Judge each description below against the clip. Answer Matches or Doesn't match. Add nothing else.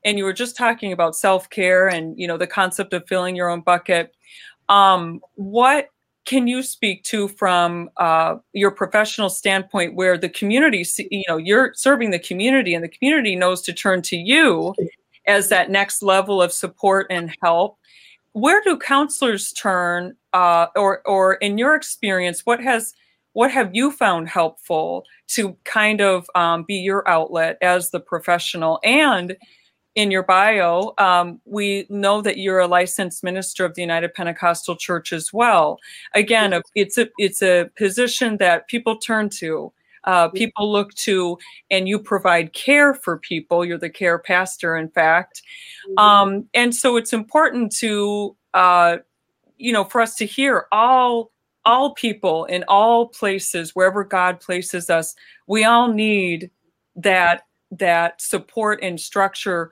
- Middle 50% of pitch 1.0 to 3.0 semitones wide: Doesn't match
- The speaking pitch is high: Matches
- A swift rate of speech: Doesn't match